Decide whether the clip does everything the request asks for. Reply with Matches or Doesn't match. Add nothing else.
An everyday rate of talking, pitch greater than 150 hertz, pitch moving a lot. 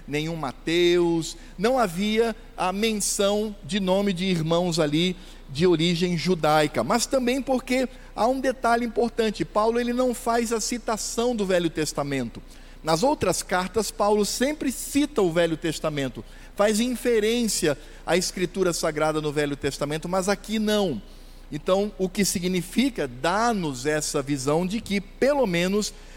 Matches